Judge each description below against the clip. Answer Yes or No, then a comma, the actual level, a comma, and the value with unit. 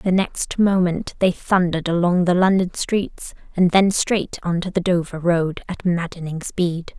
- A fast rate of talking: No, average, 170 wpm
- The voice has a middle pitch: Yes, medium, 175 Hz